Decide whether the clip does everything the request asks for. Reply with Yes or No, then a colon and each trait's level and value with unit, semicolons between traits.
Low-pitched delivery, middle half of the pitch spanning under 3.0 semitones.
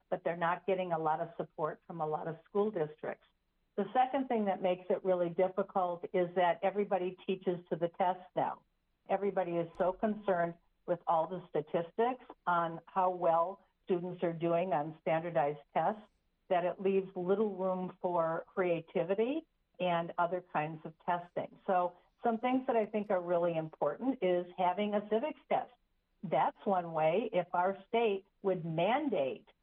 No: medium, 180 Hz; narrow, 2.4 semitones